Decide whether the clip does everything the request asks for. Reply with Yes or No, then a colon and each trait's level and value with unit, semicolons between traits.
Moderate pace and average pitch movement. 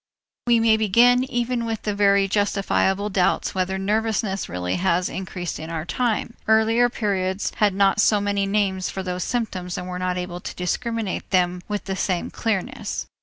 Yes: average, 170 wpm; average, 3.2 semitones